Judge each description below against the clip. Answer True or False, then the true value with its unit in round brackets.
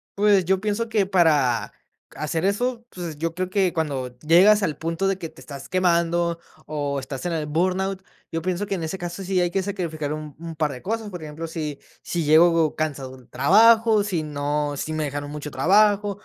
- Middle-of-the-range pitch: True (170 Hz)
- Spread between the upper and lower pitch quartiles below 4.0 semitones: False (4.3 semitones)